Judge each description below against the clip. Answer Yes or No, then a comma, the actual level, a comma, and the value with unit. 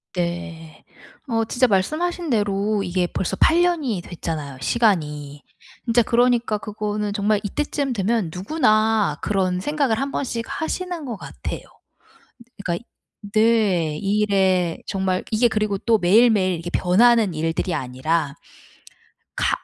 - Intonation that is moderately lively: Yes, average, 4.8 semitones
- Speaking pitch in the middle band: No, high, 205 Hz